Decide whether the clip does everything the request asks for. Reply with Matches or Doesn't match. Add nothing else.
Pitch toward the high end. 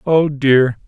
Doesn't match